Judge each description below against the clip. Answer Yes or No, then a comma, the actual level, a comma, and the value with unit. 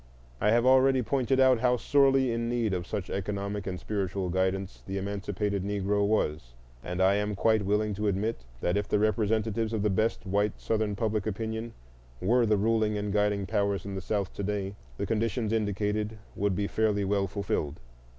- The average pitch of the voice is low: Yes, low, 105 Hz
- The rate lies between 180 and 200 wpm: Yes, average, 185 wpm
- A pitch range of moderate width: No, narrow, 2.1 semitones